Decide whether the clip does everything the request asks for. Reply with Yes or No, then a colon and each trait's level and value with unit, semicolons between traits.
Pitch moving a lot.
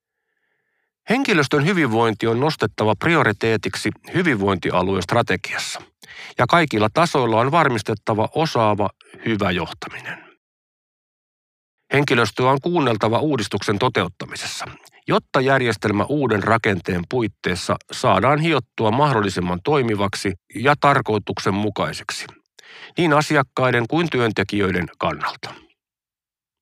Yes: wide, 5.8 semitones